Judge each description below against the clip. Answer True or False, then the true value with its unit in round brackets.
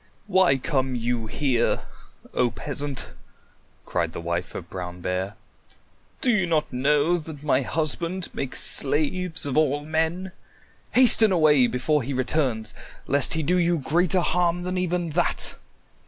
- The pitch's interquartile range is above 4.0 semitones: True (5.4 semitones)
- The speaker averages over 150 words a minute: False (140 wpm)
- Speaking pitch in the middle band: True (150 Hz)